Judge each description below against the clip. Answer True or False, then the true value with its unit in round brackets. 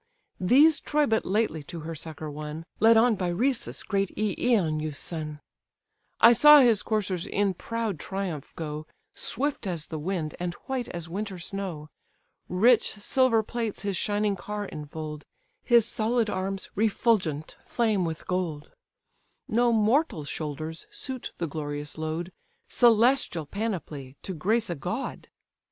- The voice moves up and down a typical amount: False (6.2 semitones)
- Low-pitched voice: False (195 Hz)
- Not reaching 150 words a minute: True (140 wpm)